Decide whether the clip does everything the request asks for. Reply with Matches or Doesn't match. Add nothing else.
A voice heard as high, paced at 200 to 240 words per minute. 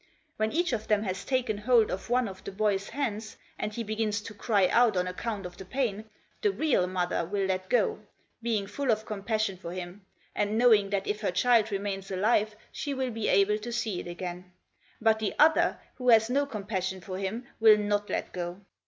Matches